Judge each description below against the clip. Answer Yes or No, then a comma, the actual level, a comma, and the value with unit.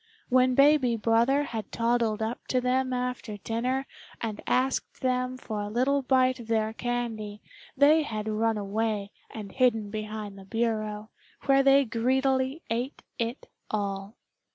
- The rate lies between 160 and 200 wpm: No, average, 145 wpm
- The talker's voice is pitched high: Yes, high, 235 Hz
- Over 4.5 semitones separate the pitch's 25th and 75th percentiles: No, average, 3.1 semitones